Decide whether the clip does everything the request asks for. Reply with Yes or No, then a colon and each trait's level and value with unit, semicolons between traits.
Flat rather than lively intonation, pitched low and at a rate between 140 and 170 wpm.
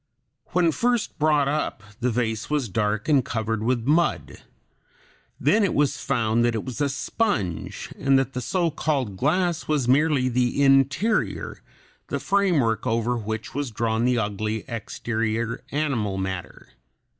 No: average, 5.0 semitones; low, 125 Hz; average, 145 wpm